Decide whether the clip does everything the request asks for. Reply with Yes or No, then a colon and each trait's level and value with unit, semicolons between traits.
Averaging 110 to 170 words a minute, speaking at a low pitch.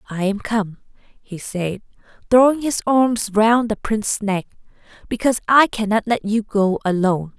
No: average, 155 wpm; high, 215 Hz